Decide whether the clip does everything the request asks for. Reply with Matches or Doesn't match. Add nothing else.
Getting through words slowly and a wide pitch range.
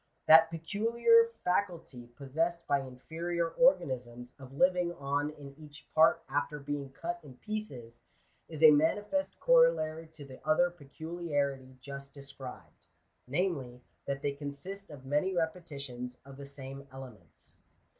Doesn't match